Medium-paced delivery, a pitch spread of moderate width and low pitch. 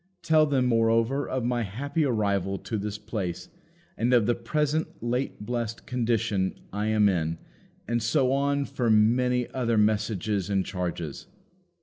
Yes: average, 145 wpm; average, 3.3 semitones; low, 115 Hz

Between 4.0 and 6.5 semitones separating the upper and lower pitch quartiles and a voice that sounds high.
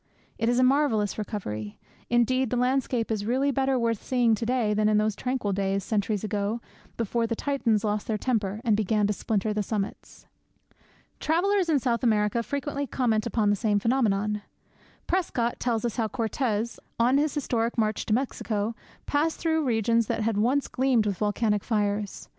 No: average, 3.3 semitones; high, 225 Hz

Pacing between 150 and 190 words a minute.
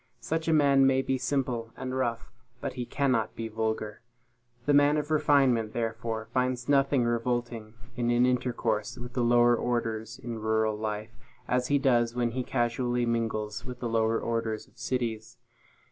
Yes: average, 165 wpm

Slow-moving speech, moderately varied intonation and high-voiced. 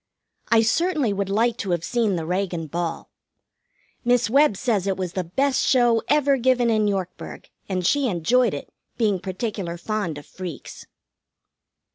No: average, 155 wpm; average, 5.0 semitones; high, 210 Hz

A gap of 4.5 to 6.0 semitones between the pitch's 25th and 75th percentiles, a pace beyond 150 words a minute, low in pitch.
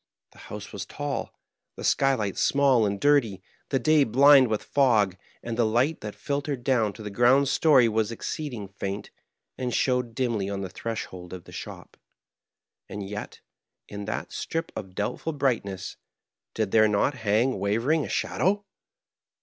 Yes: average, 5.0 semitones; average, 160 wpm; low, 115 Hz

